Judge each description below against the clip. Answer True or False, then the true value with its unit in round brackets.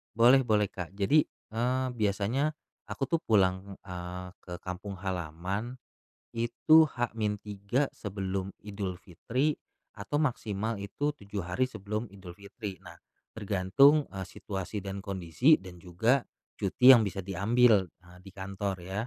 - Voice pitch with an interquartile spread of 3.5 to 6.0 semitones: True (3.9 semitones)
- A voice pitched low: True (100 Hz)